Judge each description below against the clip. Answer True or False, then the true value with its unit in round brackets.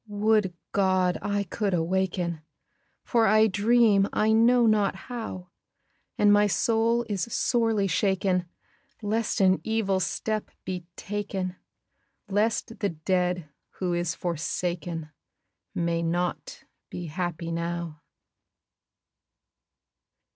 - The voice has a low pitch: False (190 Hz)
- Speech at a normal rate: False (105 wpm)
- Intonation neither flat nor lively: True (3.5 semitones)